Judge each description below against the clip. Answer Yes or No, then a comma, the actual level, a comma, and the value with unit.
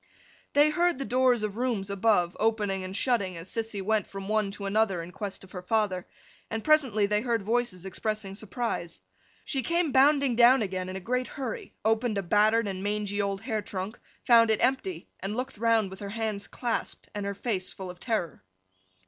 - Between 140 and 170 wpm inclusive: No, average, 195 wpm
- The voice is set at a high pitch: Yes, high, 215 Hz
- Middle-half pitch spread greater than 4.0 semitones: No, average, 3.5 semitones